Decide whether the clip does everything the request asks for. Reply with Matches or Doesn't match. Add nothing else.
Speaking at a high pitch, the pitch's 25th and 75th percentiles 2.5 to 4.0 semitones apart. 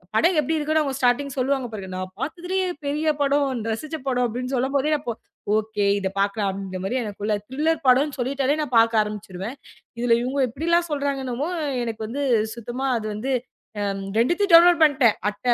Doesn't match